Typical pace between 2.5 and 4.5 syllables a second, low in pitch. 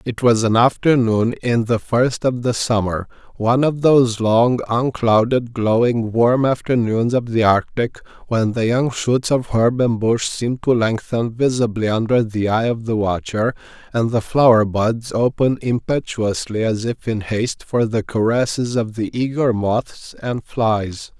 Yes: 4.2 syllables/s; low, 115 Hz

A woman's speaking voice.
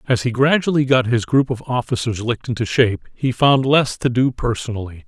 No: male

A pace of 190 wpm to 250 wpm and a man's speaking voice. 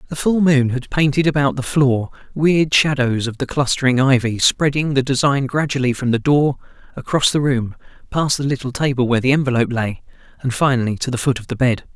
Yes: average, 200 wpm; male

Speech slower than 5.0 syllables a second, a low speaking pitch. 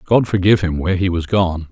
No: 6.2 syllables/s; very low, 90 Hz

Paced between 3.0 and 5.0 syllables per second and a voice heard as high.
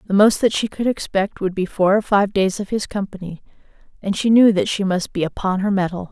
No: 5.6 syllables/s; high, 195 Hz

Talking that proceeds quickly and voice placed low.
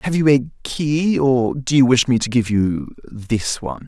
Yes: fast, 215 wpm; low, 130 Hz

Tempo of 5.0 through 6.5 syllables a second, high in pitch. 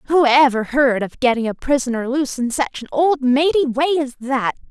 Yes: 5.2 syllables/s; very high, 265 Hz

